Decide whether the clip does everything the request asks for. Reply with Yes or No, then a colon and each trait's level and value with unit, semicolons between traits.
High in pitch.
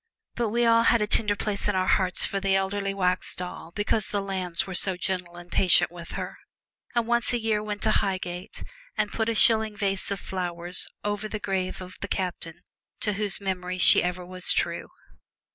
Yes: high, 195 Hz